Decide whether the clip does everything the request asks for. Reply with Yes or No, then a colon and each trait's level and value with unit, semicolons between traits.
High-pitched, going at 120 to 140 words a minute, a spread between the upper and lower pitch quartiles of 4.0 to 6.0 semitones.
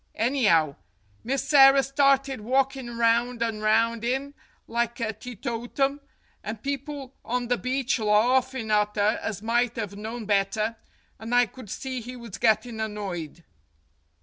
No: high, 235 Hz; slow, 135 wpm; average, 3.3 semitones